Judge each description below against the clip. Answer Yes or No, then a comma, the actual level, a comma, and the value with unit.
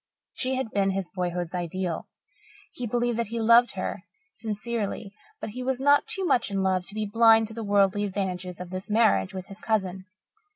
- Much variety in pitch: No, average, 3.6 semitones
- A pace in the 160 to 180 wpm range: No, average, 195 wpm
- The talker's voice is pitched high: Yes, high, 205 Hz